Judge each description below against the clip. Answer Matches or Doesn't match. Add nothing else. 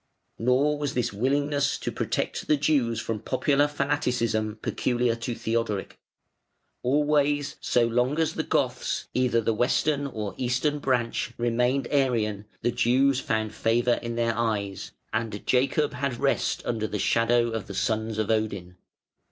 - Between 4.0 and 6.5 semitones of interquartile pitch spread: Doesn't match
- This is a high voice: Doesn't match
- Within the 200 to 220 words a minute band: Doesn't match